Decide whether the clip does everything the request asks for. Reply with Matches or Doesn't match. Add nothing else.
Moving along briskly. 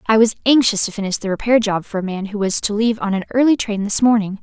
Matches